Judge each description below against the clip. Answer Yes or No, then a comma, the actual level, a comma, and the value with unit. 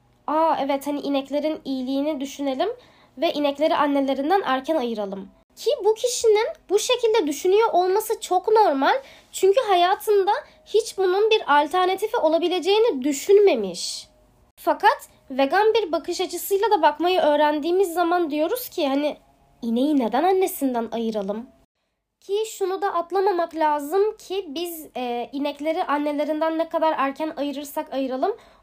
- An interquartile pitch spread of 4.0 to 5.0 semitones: No, wide, 5.5 semitones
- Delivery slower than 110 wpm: No, average, 125 wpm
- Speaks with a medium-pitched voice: No, very high, 330 Hz